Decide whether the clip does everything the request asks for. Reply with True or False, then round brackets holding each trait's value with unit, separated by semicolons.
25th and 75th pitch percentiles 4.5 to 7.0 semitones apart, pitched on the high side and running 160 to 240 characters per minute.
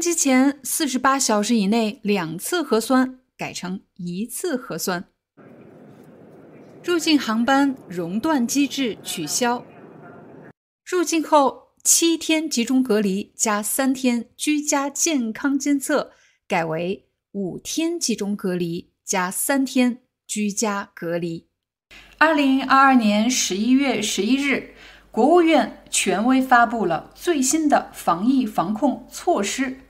True (5.3 semitones; 255 Hz; 180 characters per minute)